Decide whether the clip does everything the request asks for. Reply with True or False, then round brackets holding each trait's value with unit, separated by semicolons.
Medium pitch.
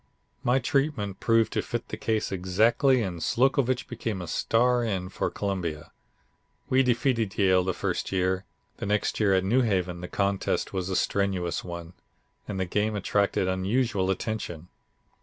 False (100 Hz)